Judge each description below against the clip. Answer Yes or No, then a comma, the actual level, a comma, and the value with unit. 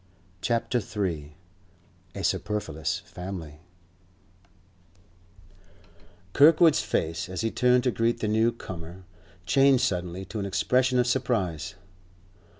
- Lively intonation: Yes, wide, 5.7 semitones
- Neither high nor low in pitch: No, low, 105 Hz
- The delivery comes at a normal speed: No, slow, 105 wpm